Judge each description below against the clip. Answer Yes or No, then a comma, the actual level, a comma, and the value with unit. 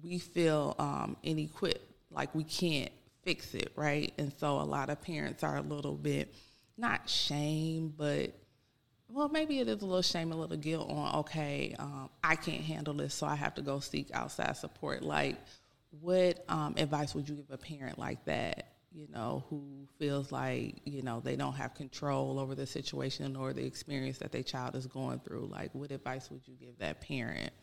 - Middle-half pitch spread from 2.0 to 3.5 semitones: Yes, average, 3.0 semitones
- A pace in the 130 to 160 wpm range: No, average, 195 wpm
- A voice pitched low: No, medium, 145 Hz